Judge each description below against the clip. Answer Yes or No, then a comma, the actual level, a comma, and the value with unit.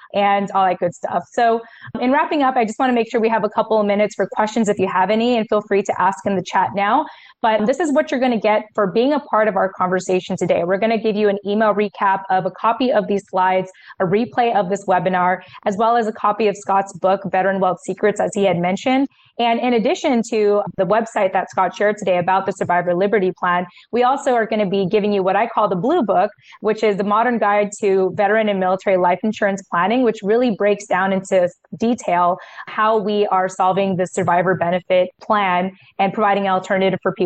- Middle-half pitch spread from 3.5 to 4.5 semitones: No, average, 2.9 semitones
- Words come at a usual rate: No, fast, 235 wpm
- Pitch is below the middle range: No, high, 205 Hz